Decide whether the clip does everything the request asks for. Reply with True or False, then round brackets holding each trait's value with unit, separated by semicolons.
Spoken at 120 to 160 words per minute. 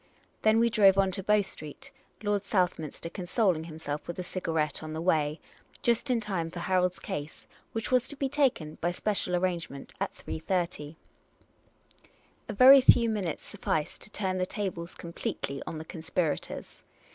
False (170 wpm)